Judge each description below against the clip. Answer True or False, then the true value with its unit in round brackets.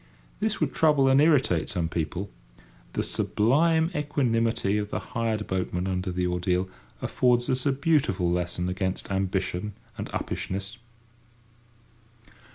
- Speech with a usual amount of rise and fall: False (6.5 semitones)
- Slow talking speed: True (125 wpm)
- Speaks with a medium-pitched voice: False (105 Hz)